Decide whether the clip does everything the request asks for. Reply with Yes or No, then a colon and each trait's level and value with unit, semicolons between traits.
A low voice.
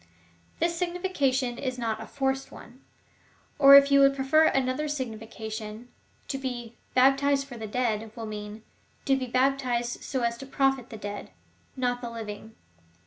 No: very high, 255 Hz